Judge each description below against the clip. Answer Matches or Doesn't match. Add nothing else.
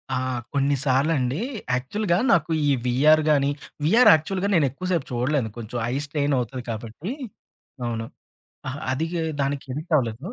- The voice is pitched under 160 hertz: Matches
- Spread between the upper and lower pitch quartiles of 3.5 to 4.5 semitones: Matches